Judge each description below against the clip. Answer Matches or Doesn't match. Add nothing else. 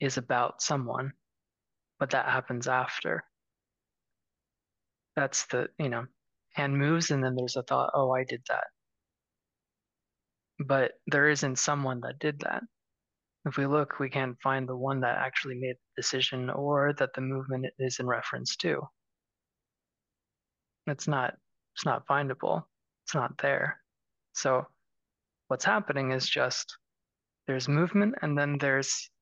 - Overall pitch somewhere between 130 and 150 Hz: Matches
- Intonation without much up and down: Matches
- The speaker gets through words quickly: Doesn't match